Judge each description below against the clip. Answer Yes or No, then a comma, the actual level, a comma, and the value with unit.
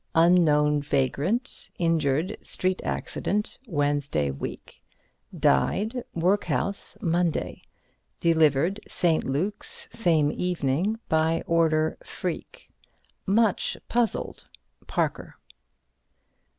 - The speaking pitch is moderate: Yes, medium, 165 Hz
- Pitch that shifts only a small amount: No, average, 4.4 semitones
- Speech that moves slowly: Yes, slow, 75 wpm